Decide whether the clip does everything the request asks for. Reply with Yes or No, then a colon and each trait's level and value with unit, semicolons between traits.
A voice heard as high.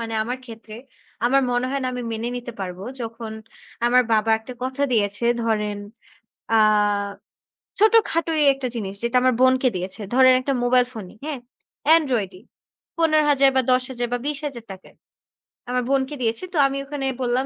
Yes: very high, 250 Hz